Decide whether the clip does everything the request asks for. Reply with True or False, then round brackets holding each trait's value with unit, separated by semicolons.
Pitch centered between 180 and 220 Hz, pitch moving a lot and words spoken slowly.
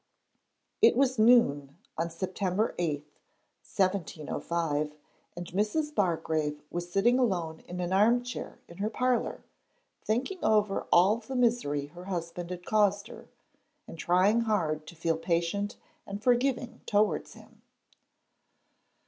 False (190 Hz; 5.0 semitones; 125 wpm)